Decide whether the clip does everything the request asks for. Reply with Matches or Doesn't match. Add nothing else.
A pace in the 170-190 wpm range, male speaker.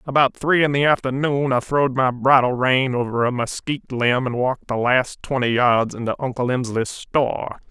Matches